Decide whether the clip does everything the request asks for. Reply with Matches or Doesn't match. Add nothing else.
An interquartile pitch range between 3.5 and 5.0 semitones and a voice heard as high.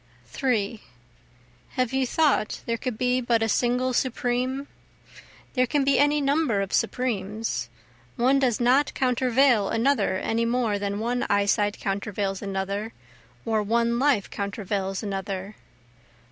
Matches